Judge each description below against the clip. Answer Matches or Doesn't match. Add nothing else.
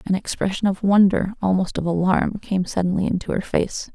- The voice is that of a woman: Matches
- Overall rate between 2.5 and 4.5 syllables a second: Doesn't match